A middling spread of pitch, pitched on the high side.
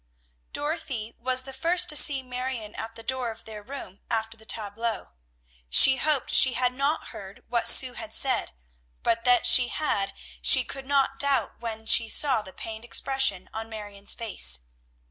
Yes: average, 3.4 semitones; high, 240 Hz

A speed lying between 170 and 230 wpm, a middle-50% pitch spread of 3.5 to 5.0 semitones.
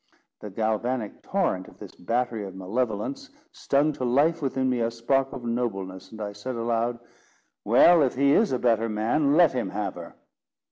Yes: average, 180 wpm; average, 4.0 semitones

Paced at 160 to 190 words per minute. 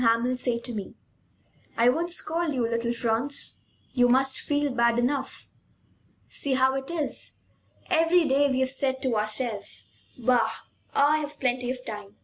No: average, 150 wpm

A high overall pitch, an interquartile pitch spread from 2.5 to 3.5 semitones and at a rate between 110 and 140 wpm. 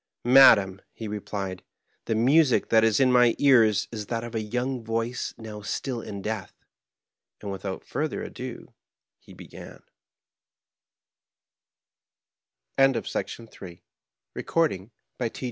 No: low, 115 Hz; average, 3.2 semitones; slow, 135 wpm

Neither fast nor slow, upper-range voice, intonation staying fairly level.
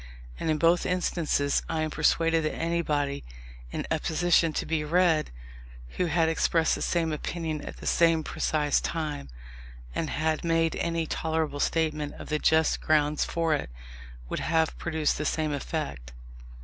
No: average, 160 wpm; medium, 160 Hz; narrow, 1.5 semitones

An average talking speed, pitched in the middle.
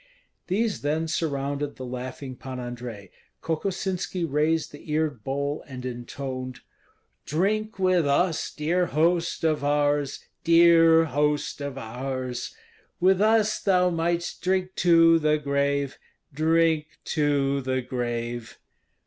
No: slow, 115 wpm; medium, 150 Hz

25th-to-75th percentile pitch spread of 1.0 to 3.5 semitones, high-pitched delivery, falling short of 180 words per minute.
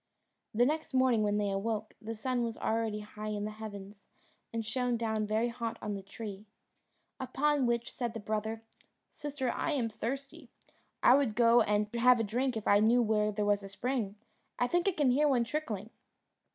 No: average, 2.9 semitones; high, 225 Hz; average, 190 wpm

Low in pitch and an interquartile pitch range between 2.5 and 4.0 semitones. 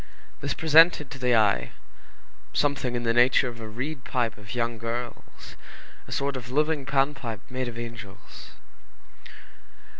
Yes: low, 125 Hz; average, 3.1 semitones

